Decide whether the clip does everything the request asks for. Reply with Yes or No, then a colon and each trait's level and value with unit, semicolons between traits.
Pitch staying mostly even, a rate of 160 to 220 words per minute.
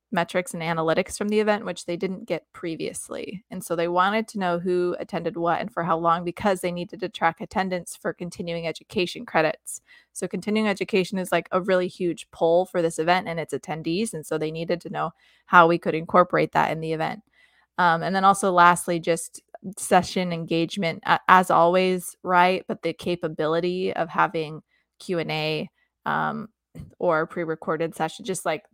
Yes: narrow, 2.1 semitones; average, 185 wpm